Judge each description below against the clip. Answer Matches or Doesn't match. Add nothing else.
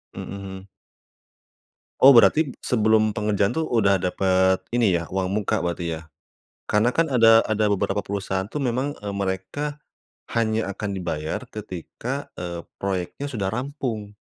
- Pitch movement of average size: Matches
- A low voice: Matches